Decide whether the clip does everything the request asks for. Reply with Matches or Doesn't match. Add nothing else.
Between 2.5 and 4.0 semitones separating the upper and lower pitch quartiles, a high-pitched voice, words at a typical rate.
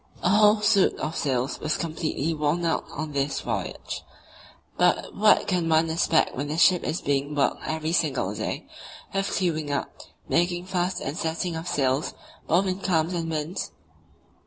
Doesn't match